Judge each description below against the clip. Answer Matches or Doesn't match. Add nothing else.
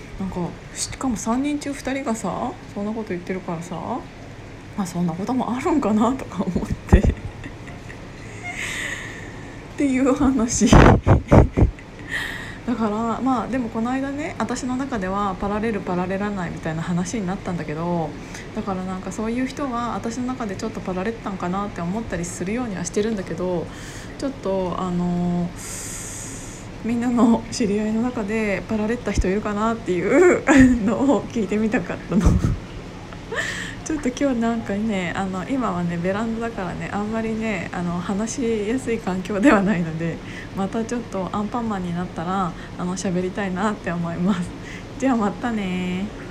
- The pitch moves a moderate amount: Matches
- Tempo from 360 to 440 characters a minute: Doesn't match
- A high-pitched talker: Matches